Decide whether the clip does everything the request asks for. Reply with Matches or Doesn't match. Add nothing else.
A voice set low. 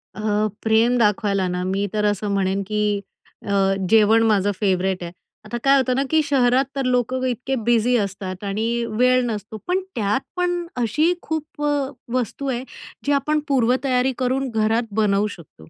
Doesn't match